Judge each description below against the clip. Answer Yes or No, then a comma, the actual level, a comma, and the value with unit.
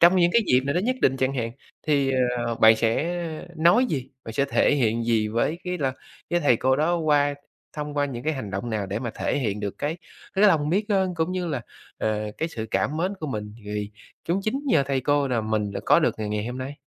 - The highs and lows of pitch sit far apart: Yes, wide, 6.5 semitones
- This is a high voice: No, low, 135 Hz